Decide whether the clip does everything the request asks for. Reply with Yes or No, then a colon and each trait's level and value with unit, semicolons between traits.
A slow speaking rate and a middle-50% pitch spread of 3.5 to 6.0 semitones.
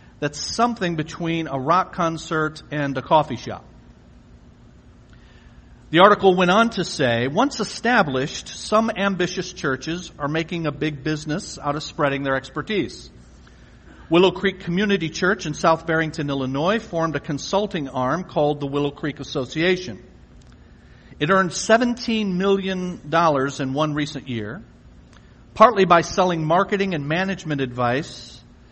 Yes: slow, 130 wpm; average, 4.6 semitones